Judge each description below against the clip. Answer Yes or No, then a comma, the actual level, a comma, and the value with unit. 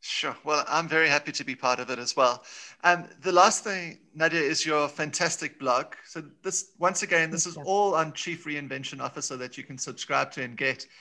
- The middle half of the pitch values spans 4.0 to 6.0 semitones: No, average, 3.5 semitones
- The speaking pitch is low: No, medium, 160 Hz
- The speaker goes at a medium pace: No, fast, 220 wpm